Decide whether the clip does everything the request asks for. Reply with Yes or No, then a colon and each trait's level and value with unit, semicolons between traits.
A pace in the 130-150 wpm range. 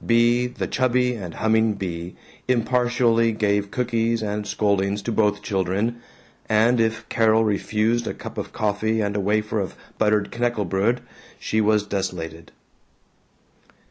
Yes: slow, 135 wpm